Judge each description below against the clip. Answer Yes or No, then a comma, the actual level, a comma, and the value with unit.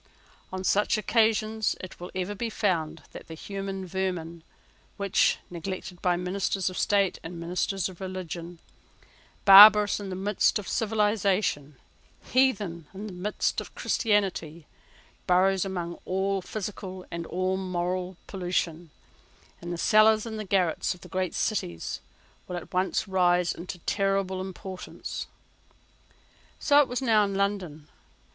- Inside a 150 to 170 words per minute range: No, slow, 135 wpm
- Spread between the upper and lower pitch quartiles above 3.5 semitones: No, narrow, 2.5 semitones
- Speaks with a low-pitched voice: No, high, 190 Hz